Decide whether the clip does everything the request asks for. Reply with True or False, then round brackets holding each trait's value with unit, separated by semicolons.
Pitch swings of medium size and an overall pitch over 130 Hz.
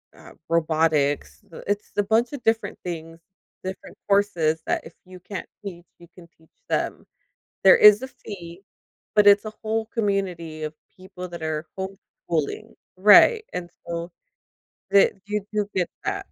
True (3.6 semitones; 185 Hz)